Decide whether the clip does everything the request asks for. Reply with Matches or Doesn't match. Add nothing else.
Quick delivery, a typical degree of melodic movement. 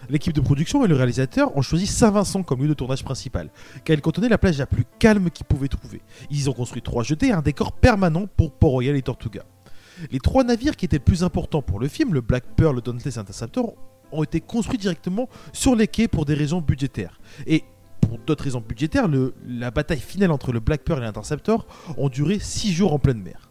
Doesn't match